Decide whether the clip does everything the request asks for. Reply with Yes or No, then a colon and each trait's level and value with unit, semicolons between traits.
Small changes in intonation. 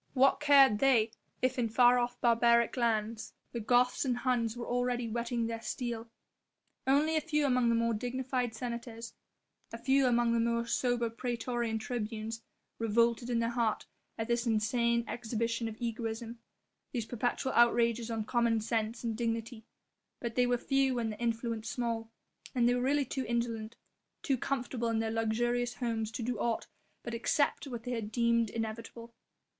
Yes: narrow, 1.4 semitones